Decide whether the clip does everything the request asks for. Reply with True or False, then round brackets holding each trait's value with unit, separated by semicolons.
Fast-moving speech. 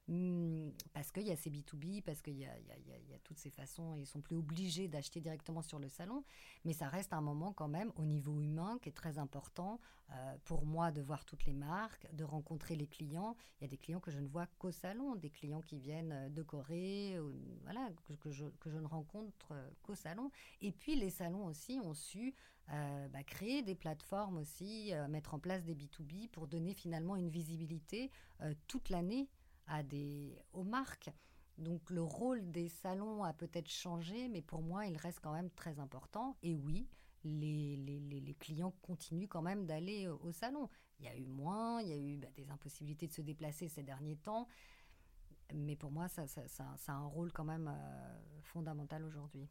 True (210 wpm)